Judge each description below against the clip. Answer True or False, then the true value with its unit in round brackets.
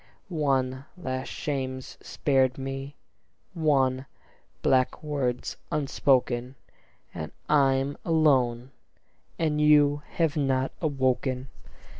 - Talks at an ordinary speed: False (85 wpm)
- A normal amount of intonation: False (2.1 semitones)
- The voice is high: False (135 Hz)